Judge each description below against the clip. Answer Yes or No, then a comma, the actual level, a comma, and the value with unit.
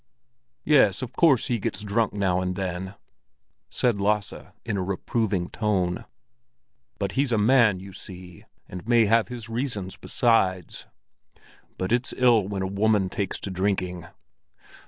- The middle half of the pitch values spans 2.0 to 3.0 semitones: No, average, 3.8 semitones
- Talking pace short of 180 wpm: Yes, average, 145 wpm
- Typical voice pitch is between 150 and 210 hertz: No, low, 100 Hz